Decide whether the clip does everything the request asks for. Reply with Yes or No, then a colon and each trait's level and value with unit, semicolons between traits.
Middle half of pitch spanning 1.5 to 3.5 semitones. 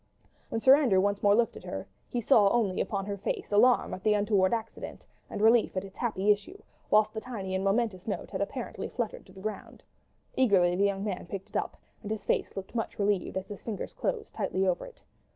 Yes: average, 2.8 semitones